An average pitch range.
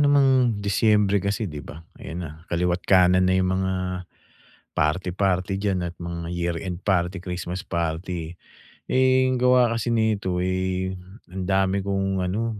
No: narrow, 2.3 semitones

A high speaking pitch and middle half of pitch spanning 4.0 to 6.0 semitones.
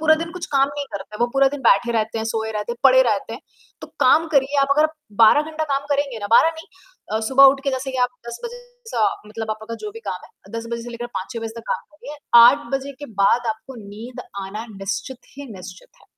Yes: very high, 250 Hz; average, 4.3 semitones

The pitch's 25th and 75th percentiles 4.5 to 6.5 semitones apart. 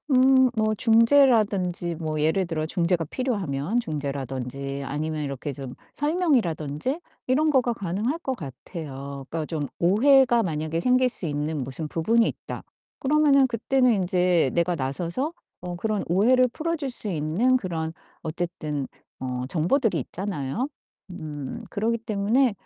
No: wide, 8.1 semitones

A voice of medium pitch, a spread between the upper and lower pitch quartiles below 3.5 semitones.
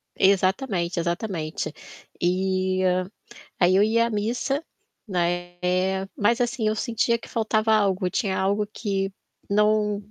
No: high, 200 Hz; average, 2.7 semitones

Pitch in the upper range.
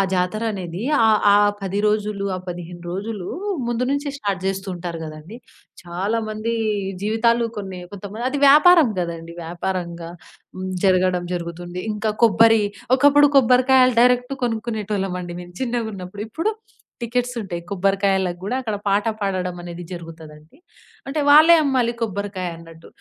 Yes: high, 200 Hz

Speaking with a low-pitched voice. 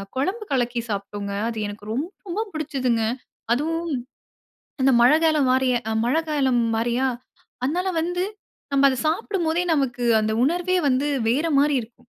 No: very high, 275 Hz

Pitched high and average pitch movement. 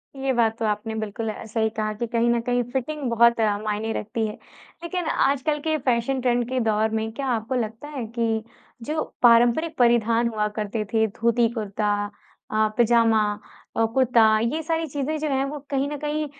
Yes: high, 235 Hz; average, 3.4 semitones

